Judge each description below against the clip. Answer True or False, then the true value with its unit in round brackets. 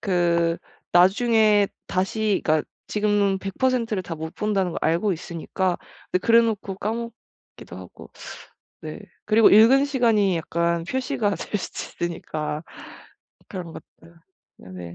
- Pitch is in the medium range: False (195 Hz)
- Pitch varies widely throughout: False (4.3 semitones)